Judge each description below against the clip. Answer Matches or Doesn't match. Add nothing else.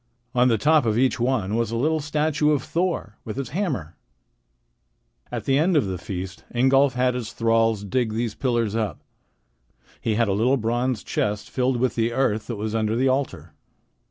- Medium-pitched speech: Doesn't match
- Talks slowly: Doesn't match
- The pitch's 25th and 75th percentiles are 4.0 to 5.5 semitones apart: Doesn't match